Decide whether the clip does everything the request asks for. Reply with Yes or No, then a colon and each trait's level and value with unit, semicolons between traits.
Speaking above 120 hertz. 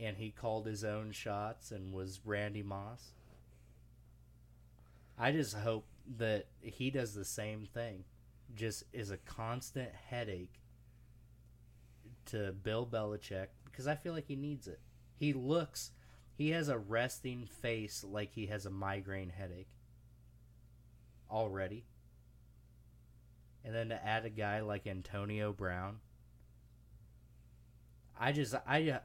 No: low, 105 Hz